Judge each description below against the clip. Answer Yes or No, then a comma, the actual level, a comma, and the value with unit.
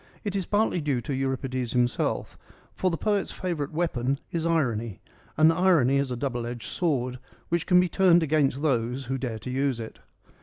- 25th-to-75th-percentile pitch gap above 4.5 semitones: Yes, average, 5.1 semitones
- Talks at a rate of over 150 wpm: Yes, average, 185 wpm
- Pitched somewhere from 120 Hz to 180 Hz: Yes, medium, 140 Hz